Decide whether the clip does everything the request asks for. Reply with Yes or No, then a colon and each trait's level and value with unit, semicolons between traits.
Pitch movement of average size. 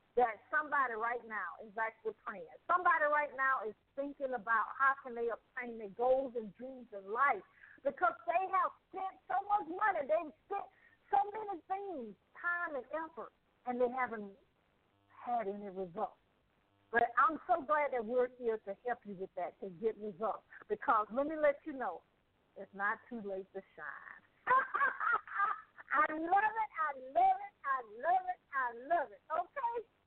No: wide, 7.7 semitones